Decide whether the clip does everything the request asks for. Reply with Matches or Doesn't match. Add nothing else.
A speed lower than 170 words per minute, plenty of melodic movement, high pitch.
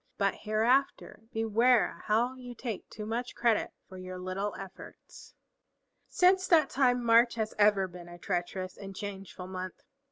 Doesn't match